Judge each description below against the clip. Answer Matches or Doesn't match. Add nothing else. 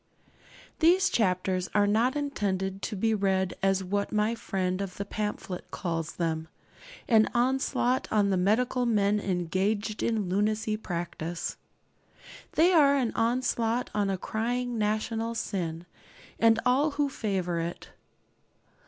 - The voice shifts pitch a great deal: Doesn't match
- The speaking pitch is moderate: Doesn't match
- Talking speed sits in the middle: Doesn't match